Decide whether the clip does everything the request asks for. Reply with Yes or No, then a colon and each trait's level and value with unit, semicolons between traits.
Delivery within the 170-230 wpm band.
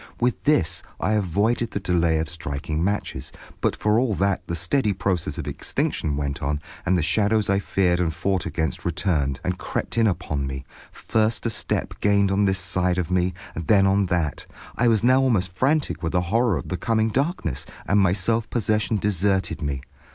Yes: average, 190 wpm